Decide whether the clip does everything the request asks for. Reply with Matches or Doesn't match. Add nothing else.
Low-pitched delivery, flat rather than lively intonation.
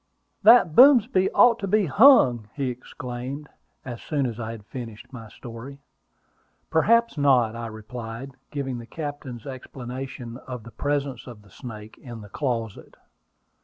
Doesn't match